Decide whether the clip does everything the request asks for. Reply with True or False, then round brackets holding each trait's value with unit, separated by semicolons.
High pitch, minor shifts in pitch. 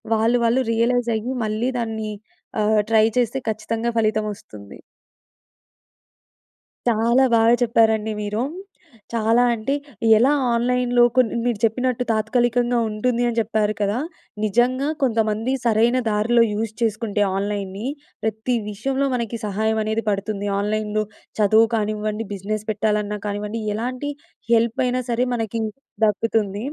True (220 Hz; 2.1 semitones)